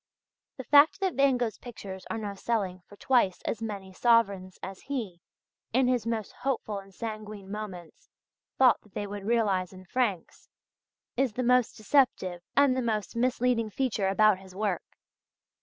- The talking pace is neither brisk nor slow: Yes, average, 160 wpm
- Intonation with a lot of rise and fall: No, average, 4.3 semitones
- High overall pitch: Yes, high, 215 Hz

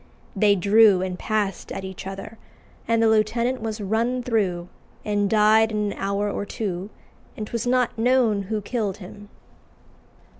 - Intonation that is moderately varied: No, narrow, 2.2 semitones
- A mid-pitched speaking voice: No, high, 210 Hz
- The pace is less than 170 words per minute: Yes, average, 155 wpm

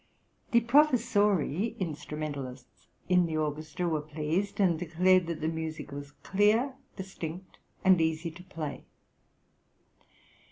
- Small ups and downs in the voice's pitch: No, average, 3.7 semitones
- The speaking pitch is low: No, medium, 170 Hz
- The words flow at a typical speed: No, slow, 115 wpm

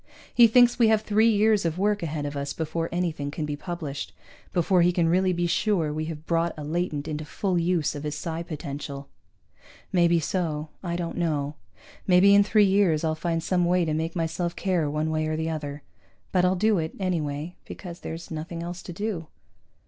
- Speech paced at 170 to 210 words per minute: Yes, average, 200 wpm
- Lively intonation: No, average, 2.9 semitones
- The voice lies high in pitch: No, medium, 170 Hz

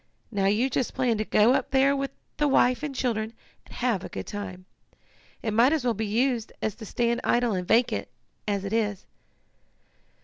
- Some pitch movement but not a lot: Yes, average, 3.4 semitones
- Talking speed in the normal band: Yes, average, 195 wpm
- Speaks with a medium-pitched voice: No, high, 230 Hz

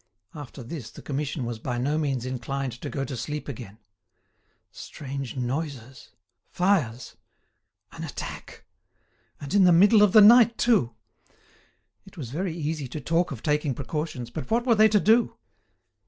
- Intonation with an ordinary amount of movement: No, wide, 5.9 semitones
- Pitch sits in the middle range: Yes, medium, 145 Hz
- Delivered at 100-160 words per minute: Yes, average, 155 wpm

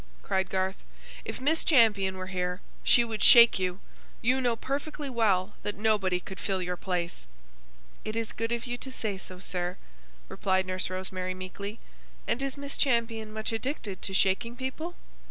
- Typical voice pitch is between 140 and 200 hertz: No, high, 210 Hz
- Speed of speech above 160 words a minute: Yes, average, 170 wpm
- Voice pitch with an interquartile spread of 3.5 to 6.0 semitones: Yes, average, 4.2 semitones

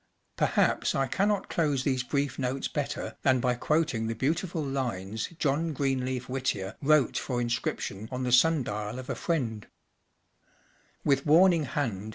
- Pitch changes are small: No, average, 3.7 semitones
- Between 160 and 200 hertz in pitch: No, low, 130 Hz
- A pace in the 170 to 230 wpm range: No, average, 160 wpm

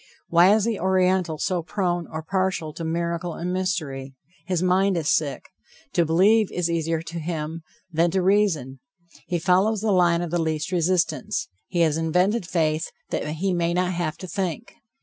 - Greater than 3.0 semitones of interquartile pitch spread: No, narrow, 2.5 semitones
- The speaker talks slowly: No, average, 175 wpm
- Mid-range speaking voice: Yes, medium, 175 Hz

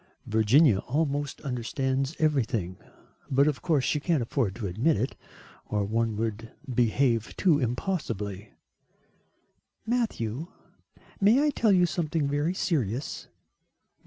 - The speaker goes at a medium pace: No, slow, 115 wpm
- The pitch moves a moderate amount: No, wide, 5.8 semitones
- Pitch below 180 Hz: Yes, low, 135 Hz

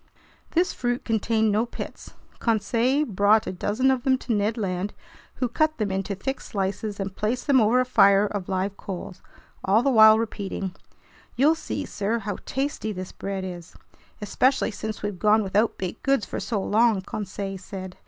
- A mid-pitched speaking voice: No, high, 215 Hz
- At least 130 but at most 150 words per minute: No, average, 175 wpm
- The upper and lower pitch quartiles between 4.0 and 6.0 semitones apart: No, average, 3.5 semitones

